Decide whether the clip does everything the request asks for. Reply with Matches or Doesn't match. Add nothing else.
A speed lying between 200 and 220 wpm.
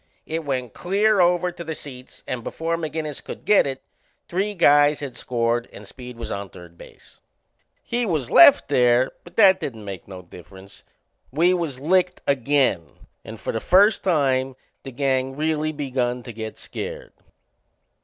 Doesn't match